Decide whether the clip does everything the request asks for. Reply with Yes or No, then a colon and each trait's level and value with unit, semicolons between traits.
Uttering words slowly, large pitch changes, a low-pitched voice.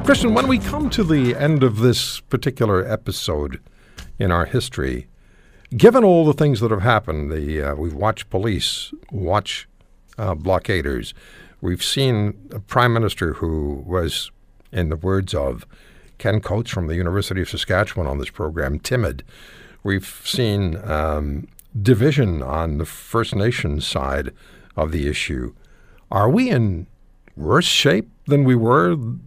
No: average, 145 wpm; wide, 7.1 semitones; low, 100 Hz